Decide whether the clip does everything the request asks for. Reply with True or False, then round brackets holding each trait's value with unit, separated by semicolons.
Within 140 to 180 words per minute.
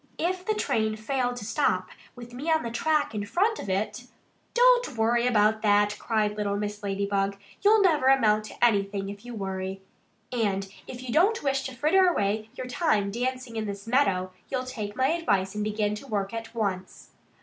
False (195 wpm)